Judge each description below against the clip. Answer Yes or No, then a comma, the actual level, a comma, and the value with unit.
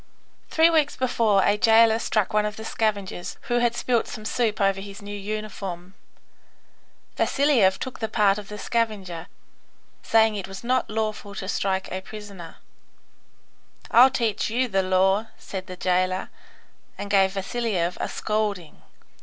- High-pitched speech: Yes, high, 210 Hz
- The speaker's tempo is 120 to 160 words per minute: Yes, average, 155 wpm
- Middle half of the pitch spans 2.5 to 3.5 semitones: Yes, average, 2.8 semitones